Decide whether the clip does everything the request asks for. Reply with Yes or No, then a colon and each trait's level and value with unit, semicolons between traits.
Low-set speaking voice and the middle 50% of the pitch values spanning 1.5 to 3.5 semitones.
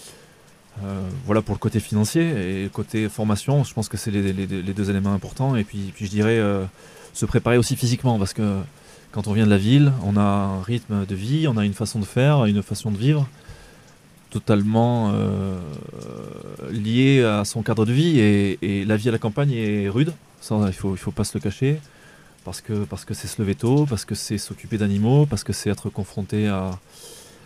Yes: low, 110 Hz; average, 3.1 semitones